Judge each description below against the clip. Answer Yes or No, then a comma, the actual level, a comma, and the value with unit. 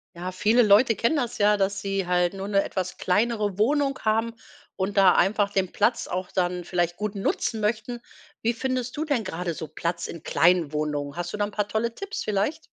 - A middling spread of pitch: Yes, average, 4.1 semitones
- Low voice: No, high, 200 Hz